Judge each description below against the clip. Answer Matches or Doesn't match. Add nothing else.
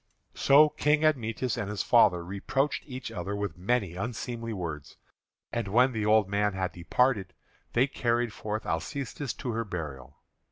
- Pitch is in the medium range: Doesn't match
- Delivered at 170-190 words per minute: Doesn't match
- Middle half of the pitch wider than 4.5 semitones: Matches